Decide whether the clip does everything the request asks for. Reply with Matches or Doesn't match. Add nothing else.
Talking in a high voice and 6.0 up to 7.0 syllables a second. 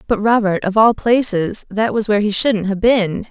Doesn't match